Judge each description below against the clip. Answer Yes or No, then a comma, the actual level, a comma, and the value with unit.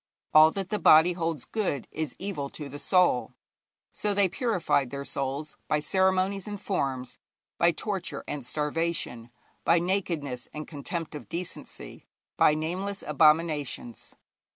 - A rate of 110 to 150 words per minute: Yes, slow, 135 wpm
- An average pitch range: Yes, average, 4.5 semitones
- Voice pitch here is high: No, medium, 160 Hz